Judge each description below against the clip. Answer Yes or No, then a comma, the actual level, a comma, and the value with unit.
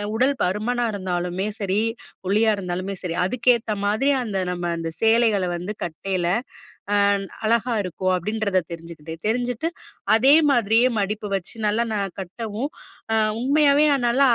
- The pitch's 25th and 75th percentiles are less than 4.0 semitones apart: No, average, 4.3 semitones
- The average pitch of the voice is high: Yes, high, 210 Hz